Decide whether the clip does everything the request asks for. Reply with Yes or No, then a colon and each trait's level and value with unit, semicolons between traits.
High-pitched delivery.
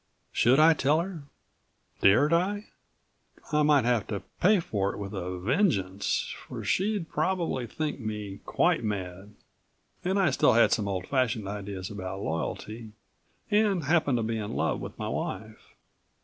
No: low, 115 Hz